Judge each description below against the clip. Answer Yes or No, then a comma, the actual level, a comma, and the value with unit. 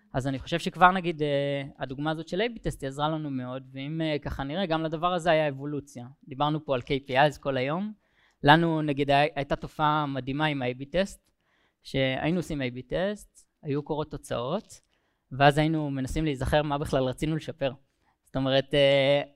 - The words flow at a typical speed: No, fast, 170 wpm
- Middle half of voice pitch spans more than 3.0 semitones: No, narrow, 2.6 semitones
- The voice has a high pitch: No, medium, 145 Hz